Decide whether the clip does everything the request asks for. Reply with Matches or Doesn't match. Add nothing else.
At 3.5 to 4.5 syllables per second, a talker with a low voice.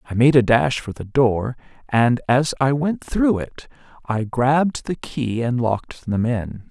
Matches